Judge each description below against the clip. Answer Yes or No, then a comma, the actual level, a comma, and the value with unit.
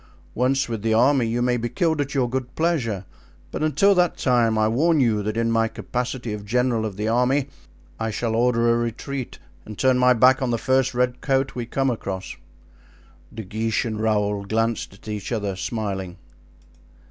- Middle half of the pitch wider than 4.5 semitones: No, average, 3.1 semitones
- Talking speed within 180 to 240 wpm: Yes, average, 190 wpm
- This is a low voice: Yes, low, 120 Hz